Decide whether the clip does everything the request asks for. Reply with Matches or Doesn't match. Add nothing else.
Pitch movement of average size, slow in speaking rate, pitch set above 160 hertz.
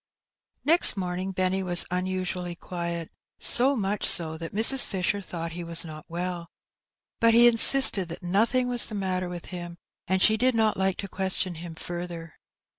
Doesn't match